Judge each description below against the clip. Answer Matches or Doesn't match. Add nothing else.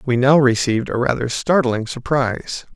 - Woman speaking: Doesn't match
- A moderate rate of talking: Matches